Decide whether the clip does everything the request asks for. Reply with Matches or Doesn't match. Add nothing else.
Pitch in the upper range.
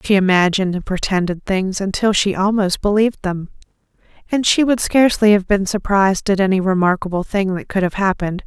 Matches